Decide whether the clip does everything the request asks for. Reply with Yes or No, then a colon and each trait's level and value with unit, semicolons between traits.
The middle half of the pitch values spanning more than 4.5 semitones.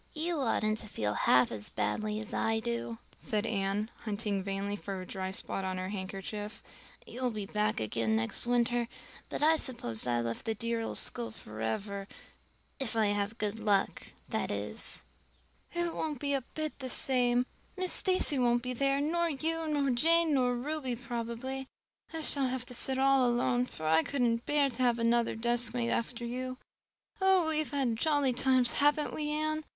Yes: average, 4.9 semitones